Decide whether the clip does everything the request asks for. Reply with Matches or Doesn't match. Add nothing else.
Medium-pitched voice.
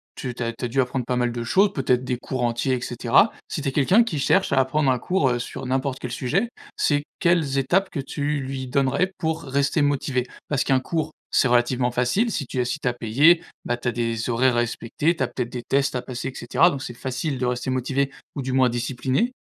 Doesn't match